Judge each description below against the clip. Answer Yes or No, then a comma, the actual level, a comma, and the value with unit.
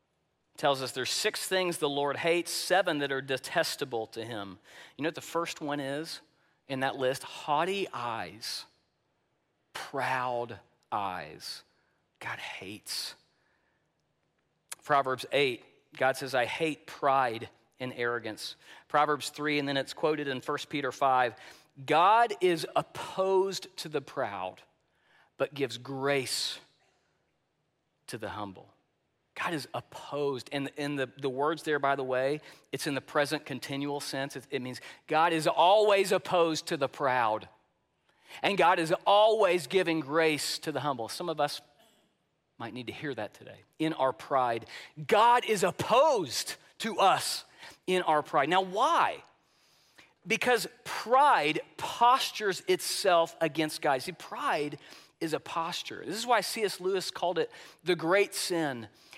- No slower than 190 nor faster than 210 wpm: No, average, 140 wpm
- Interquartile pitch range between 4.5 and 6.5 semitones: Yes, average, 4.8 semitones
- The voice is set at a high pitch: No, medium, 150 Hz